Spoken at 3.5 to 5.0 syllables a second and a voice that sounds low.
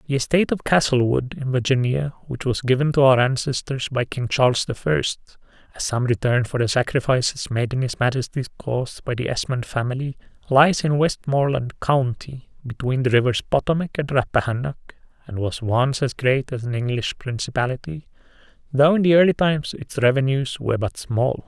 No: 5.4 syllables/s; low, 130 Hz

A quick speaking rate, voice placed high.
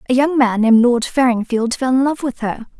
Yes: fast, 235 wpm; very high, 250 Hz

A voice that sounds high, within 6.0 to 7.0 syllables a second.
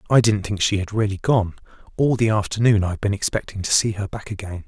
No: low, 105 Hz; 6.2 syllables/s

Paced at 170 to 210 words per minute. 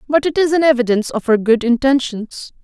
Yes: fast, 205 wpm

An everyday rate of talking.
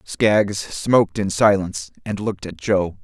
Yes: average, 160 wpm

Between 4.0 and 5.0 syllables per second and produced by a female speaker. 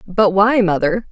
Yes: 4.1 syllables/s; female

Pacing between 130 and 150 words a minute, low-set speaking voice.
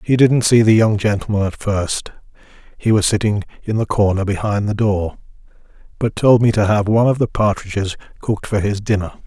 No: average, 180 wpm; low, 105 Hz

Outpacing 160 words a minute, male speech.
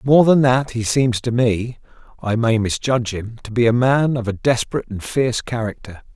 Yes: fast, 205 wpm; male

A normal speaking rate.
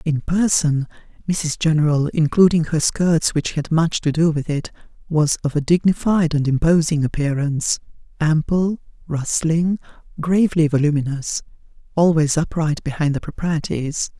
No: slow, 125 wpm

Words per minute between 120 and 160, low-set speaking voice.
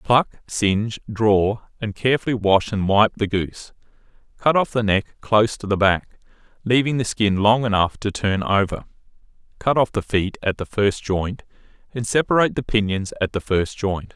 No: average, 180 wpm; low, 105 Hz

